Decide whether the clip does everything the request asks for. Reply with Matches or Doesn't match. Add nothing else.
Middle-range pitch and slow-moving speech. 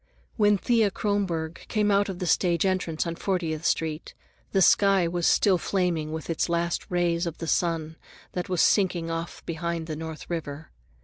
Doesn't match